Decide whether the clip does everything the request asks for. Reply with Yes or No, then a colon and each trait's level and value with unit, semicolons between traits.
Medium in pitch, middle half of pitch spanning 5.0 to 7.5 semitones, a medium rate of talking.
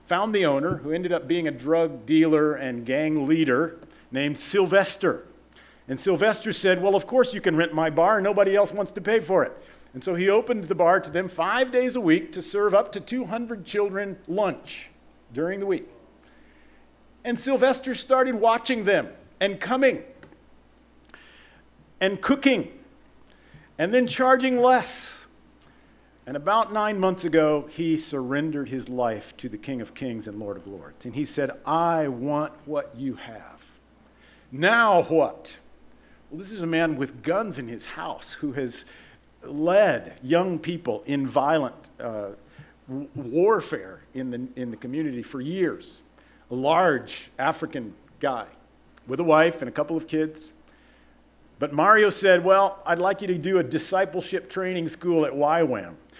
Yes: medium, 175 Hz; wide, 5.6 semitones; average, 160 wpm